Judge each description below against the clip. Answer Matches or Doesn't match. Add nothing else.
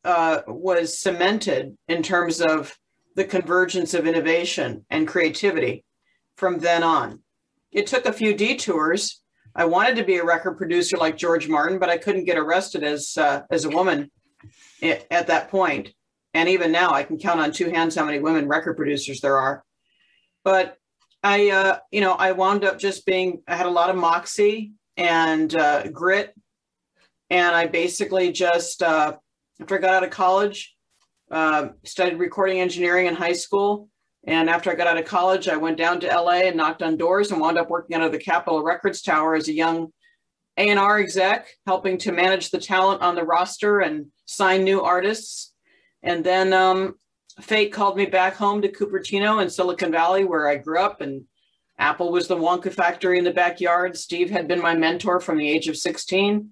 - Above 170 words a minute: Matches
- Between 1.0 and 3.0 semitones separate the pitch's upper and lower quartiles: Matches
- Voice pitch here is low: Doesn't match